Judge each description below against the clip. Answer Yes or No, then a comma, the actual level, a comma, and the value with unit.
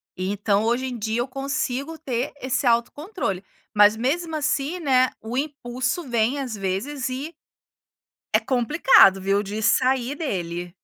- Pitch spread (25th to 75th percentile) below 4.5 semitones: No, average, 4.9 semitones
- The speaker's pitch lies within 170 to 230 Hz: No, very high, 250 Hz